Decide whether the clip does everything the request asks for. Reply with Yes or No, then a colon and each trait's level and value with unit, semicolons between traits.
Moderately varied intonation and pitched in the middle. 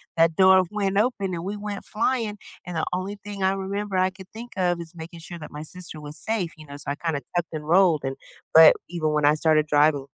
Yes: average, 3.9 semitones; medium, 175 Hz